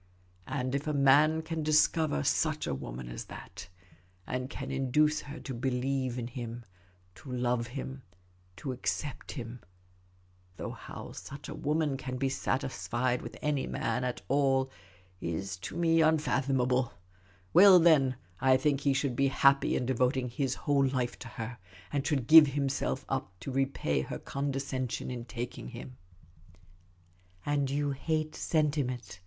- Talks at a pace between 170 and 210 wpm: No, average, 160 wpm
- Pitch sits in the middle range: No, low, 130 Hz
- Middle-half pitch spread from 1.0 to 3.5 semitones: Yes, average, 2.8 semitones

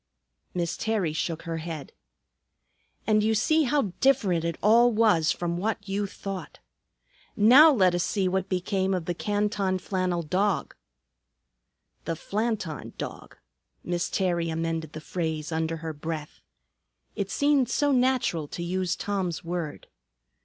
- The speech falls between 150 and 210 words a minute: No, average, 140 wpm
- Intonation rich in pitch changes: No, average, 4.1 semitones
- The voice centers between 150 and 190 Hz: Yes, medium, 185 Hz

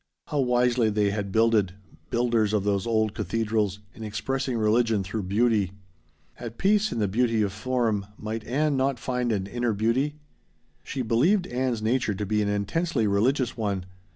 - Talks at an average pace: Yes, average, 165 wpm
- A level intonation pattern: No, average, 3.2 semitones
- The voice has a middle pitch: No, low, 115 Hz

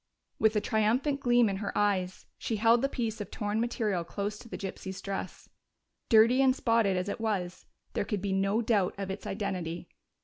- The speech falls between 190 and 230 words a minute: Yes, average, 195 wpm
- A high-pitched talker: Yes, high, 210 Hz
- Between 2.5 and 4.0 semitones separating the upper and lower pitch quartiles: Yes, average, 2.9 semitones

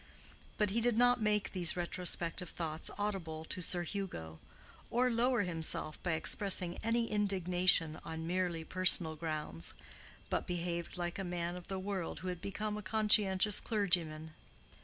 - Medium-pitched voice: Yes, medium, 180 Hz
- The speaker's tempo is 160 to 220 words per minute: No, average, 150 wpm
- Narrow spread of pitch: No, average, 3.7 semitones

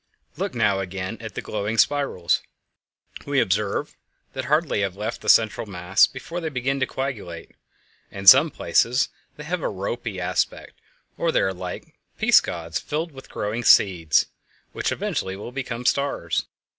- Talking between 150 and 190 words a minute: Yes, average, 155 wpm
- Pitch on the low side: Yes, low, 110 Hz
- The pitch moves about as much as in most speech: No, wide, 5.8 semitones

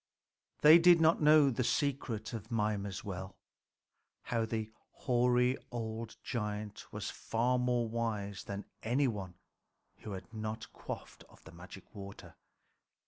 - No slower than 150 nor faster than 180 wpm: No, slow, 135 wpm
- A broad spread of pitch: No, average, 3.2 semitones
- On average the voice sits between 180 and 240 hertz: No, low, 115 Hz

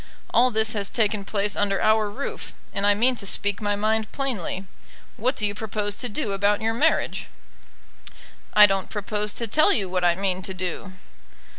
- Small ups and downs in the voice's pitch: Yes, narrow, 1.9 semitones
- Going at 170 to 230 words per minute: Yes, average, 185 wpm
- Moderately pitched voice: No, high, 205 Hz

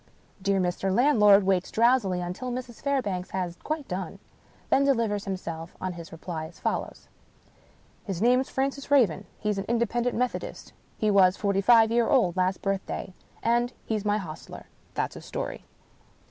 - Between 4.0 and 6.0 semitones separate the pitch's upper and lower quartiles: Yes, average, 4.7 semitones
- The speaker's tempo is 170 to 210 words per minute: No, average, 160 wpm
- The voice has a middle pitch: No, high, 205 Hz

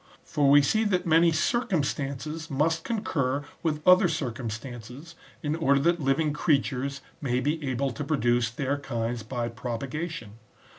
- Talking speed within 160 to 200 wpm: No, average, 150 wpm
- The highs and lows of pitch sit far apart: No, average, 4.3 semitones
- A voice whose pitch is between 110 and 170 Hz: Yes, medium, 140 Hz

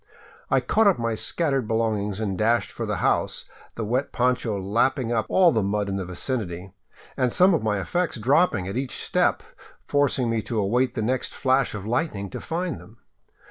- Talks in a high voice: No, low, 115 Hz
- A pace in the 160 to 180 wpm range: No, average, 195 wpm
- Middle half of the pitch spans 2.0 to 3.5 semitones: No, average, 4.3 semitones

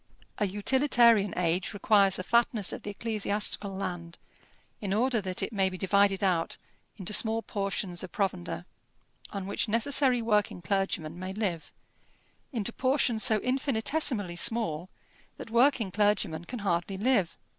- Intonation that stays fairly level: No, average, 3.6 semitones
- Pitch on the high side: Yes, high, 205 Hz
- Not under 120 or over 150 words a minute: Yes, average, 140 wpm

